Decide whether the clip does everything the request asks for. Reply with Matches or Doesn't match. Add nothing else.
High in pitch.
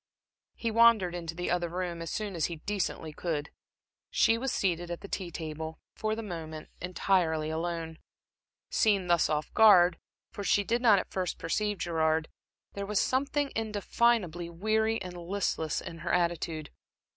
Doesn't match